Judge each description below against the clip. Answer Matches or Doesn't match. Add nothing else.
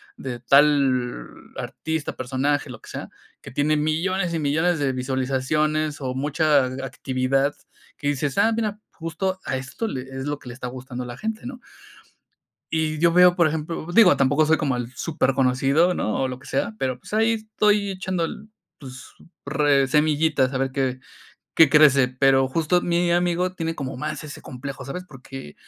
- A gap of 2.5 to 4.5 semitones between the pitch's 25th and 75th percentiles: Matches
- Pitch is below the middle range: Doesn't match